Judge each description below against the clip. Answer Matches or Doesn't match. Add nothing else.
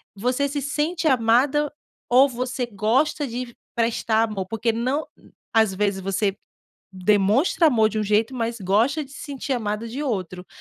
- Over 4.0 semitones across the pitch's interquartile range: Matches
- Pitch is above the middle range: Matches